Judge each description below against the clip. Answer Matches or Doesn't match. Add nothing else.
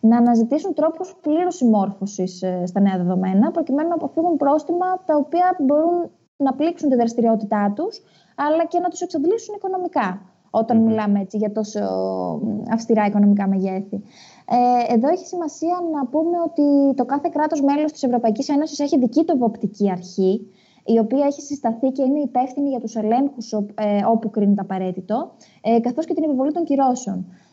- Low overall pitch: Doesn't match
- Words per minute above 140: Matches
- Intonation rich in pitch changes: Matches